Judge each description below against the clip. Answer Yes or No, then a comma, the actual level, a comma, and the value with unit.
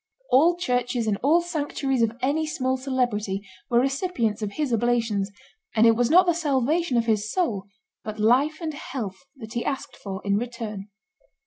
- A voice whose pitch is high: Yes, high, 245 Hz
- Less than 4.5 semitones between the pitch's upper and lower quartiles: No, average, 4.8 semitones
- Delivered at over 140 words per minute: Yes, average, 175 wpm